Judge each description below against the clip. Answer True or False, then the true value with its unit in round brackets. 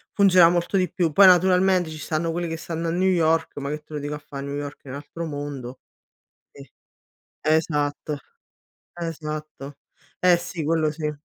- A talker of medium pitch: True (160 Hz)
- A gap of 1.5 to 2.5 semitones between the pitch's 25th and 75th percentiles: False (2.9 semitones)